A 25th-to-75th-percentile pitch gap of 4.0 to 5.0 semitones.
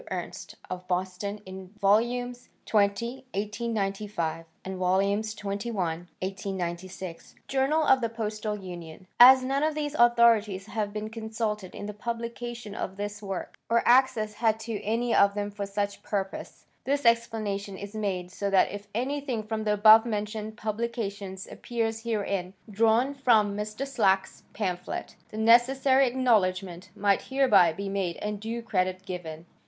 No: average, 3.1 semitones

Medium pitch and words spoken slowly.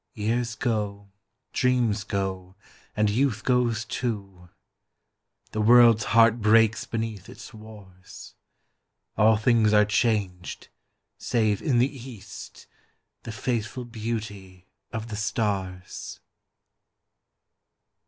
No: low, 110 Hz; slow, 95 wpm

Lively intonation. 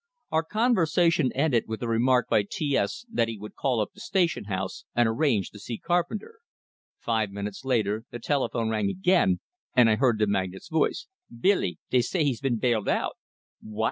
Yes: wide, 6.9 semitones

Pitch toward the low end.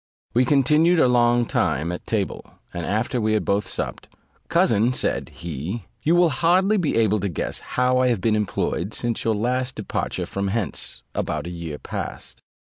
Yes: low, 115 Hz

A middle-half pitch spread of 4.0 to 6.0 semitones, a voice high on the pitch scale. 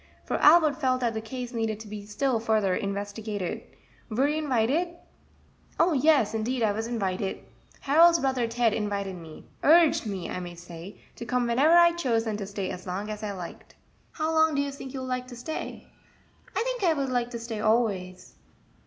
Yes: average, 5.3 semitones; high, 235 Hz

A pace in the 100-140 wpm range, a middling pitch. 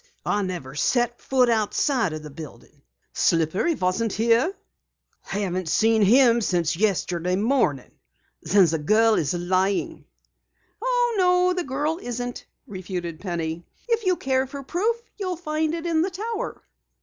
No: slow, 135 wpm; high, 225 Hz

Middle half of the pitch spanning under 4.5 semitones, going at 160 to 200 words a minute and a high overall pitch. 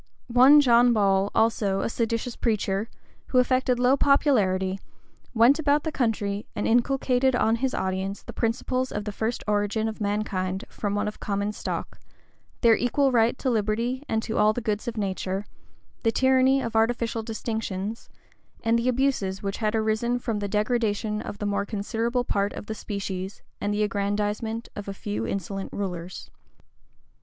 Yes: average, 3.2 semitones; average, 165 wpm; high, 220 Hz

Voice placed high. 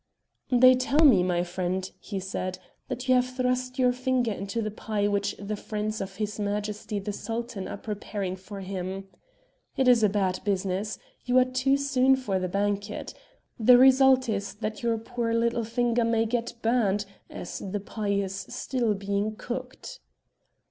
Yes: high, 215 Hz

